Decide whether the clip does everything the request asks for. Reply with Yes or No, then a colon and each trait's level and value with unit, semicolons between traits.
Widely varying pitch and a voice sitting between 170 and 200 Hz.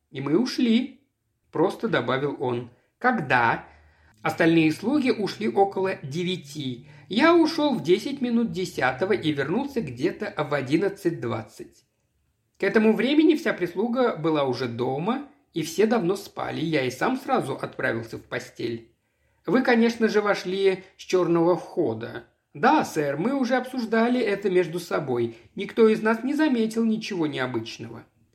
Yes: wide, 8.3 semitones; high, 190 Hz